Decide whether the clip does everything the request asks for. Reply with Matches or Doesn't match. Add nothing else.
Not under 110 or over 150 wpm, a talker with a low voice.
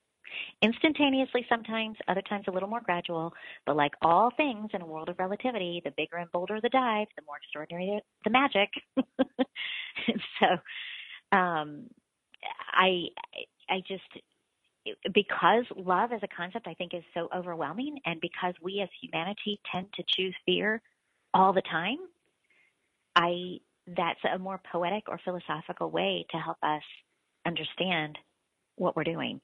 Doesn't match